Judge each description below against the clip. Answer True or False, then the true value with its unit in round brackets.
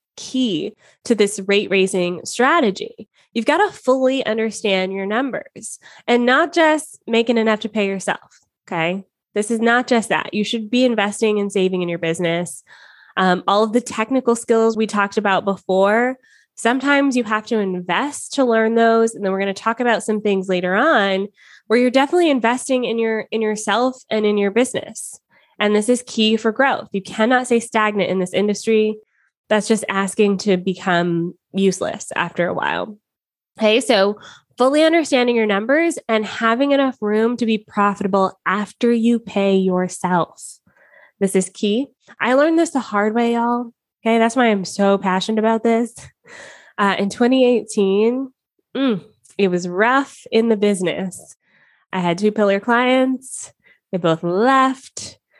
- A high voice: True (220 Hz)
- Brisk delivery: False (165 wpm)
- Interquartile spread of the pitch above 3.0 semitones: True (3.7 semitones)